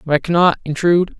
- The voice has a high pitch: No, medium, 165 Hz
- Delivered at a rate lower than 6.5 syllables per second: No, 6.8 syllables/s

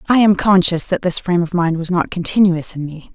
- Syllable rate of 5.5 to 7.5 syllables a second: Yes, 5.7 syllables/s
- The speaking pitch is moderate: Yes, medium, 175 Hz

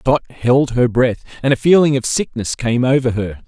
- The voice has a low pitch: Yes, low, 125 Hz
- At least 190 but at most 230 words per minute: Yes, fast, 205 wpm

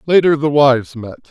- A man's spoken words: Yes, male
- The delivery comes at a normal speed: Yes, average, 185 wpm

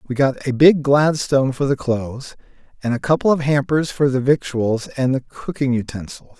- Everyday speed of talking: Yes, average, 190 wpm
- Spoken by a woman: No, male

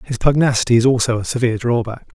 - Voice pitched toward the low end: Yes, low, 120 Hz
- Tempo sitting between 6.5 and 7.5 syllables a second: Yes, 6.9 syllables/s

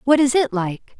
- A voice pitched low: No, very high, 250 Hz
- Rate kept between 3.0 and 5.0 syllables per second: Yes, 4.7 syllables/s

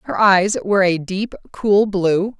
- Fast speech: No, average, 175 wpm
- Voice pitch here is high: Yes, high, 195 Hz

